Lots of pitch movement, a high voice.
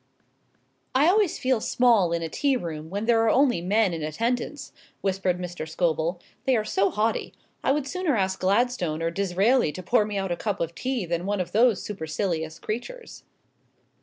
Yes: wide, 5.9 semitones; high, 200 Hz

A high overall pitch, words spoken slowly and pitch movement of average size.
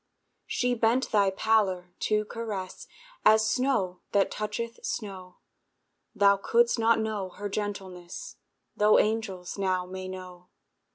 Yes: high, 205 Hz; slow, 120 wpm; average, 3.0 semitones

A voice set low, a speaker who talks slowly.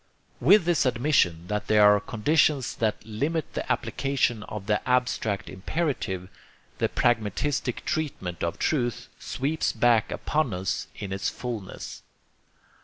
Yes: low, 115 Hz; slow, 125 wpm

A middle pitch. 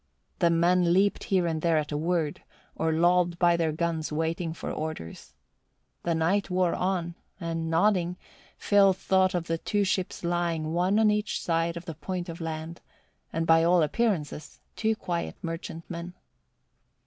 Yes: medium, 170 Hz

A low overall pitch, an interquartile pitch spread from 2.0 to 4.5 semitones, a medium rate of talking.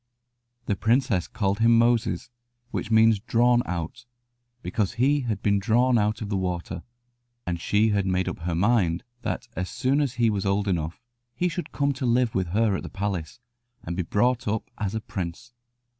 Yes: low, 110 Hz; average, 4.2 semitones; average, 190 wpm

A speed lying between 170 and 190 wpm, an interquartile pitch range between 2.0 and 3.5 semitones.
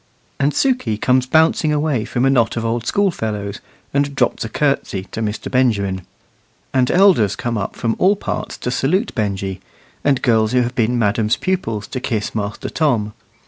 No: average, 180 wpm; average, 4.7 semitones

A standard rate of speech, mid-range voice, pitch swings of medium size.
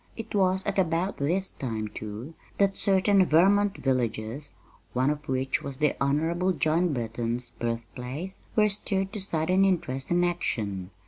No: average, 145 wpm; medium, 160 Hz; wide, 7.2 semitones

